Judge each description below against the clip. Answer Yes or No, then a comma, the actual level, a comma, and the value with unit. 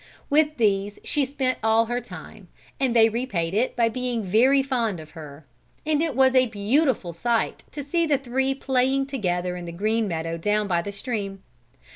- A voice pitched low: No, high, 230 Hz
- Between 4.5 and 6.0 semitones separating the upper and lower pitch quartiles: Yes, average, 5.2 semitones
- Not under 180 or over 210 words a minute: Yes, average, 185 wpm